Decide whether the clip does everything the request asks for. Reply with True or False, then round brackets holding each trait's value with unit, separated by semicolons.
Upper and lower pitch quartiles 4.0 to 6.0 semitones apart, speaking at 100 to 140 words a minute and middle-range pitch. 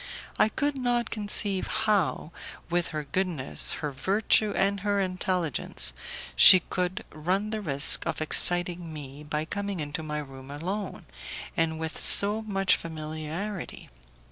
True (4.7 semitones; 135 wpm; 180 Hz)